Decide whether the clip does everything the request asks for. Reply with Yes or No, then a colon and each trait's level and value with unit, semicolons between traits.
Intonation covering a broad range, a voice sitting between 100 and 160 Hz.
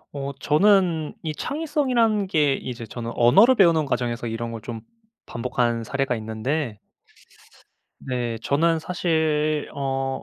Yes: wide, 5.8 semitones; medium, 140 Hz